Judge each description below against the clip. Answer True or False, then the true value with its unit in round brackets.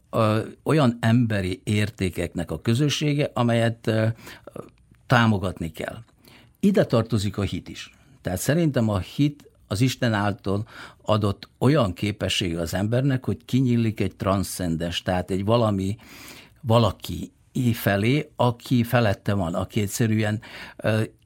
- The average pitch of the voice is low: True (110 Hz)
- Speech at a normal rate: True (115 wpm)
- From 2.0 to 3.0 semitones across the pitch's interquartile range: False (3.9 semitones)